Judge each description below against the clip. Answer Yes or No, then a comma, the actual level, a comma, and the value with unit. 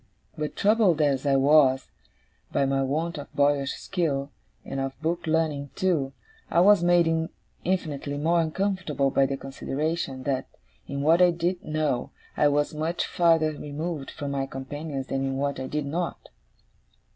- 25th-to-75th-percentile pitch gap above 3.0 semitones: Yes, average, 3.4 semitones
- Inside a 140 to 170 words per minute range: Yes, average, 155 wpm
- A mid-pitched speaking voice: Yes, medium, 150 Hz